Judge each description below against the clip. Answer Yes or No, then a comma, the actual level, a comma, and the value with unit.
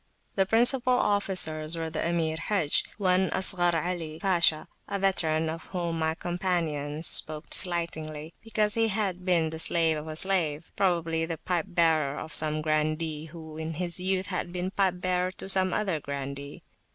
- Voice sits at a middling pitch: Yes, medium, 170 Hz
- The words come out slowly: No, average, 165 wpm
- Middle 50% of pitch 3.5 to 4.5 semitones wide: No, average, 2.9 semitones